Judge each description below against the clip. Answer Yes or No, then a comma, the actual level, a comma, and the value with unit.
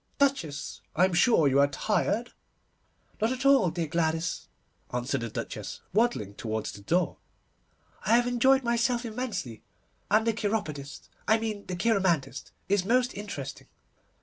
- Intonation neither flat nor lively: No, wide, 8.2 semitones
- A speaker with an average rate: Yes, average, 145 wpm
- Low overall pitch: No, high, 200 Hz